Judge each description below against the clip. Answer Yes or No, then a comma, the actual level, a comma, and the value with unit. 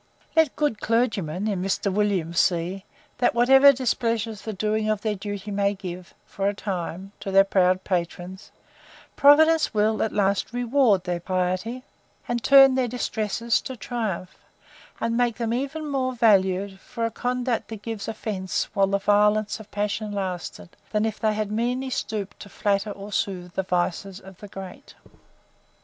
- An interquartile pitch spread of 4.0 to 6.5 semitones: No, average, 3.4 semitones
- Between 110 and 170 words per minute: Yes, average, 165 wpm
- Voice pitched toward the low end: No, high, 210 Hz